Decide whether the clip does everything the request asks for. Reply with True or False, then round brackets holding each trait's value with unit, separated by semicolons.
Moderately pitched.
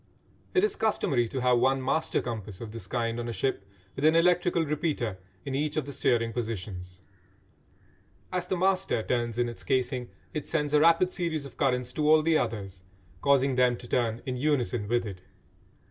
False (125 Hz)